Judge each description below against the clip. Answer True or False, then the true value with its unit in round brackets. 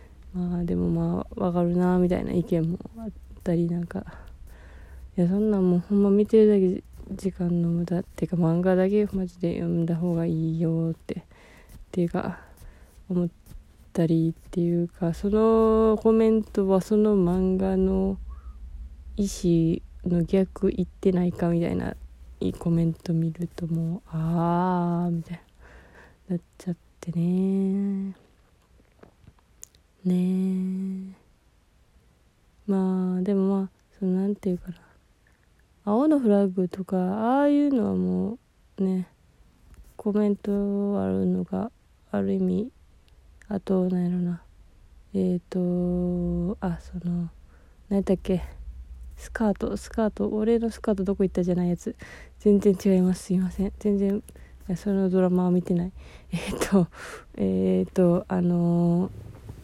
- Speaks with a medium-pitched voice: True (180 Hz)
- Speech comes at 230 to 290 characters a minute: True (260 characters per minute)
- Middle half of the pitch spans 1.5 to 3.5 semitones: True (2.7 semitones)